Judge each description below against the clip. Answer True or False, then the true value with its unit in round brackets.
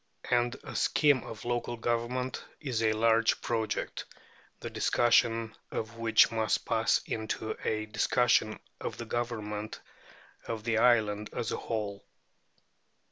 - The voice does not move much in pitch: True (1.6 semitones)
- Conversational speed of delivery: False (130 wpm)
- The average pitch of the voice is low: True (115 Hz)